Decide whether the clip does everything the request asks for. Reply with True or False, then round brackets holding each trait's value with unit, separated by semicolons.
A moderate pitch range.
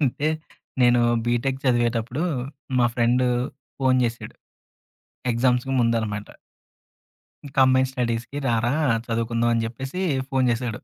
False (2.1 semitones)